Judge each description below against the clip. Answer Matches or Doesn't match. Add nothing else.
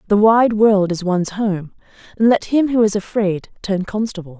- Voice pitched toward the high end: Matches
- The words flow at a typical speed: Matches